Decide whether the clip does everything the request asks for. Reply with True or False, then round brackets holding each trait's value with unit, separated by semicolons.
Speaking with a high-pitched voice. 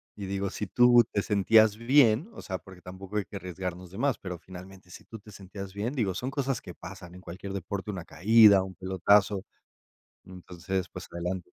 False (95 Hz)